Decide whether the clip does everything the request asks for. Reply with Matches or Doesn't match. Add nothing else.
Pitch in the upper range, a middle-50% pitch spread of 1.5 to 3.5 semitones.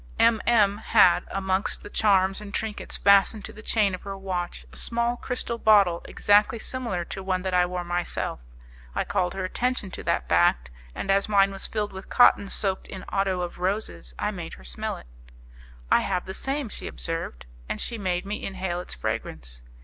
Matches